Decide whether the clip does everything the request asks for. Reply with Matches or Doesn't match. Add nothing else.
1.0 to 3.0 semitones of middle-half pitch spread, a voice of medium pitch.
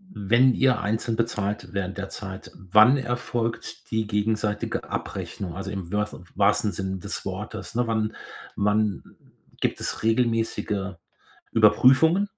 Doesn't match